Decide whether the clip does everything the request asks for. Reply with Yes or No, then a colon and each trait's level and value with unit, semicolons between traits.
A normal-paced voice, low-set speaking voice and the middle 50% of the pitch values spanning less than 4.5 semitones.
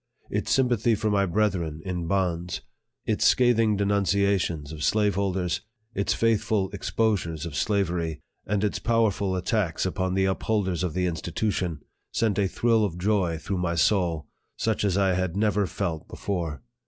Yes: average, 155 wpm; very low, 95 Hz; average, 3.3 semitones